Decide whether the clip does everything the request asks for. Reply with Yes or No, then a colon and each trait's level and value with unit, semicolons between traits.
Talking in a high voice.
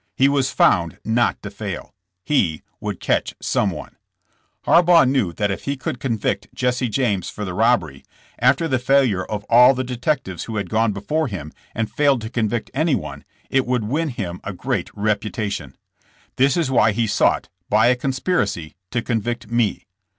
No: low, 115 Hz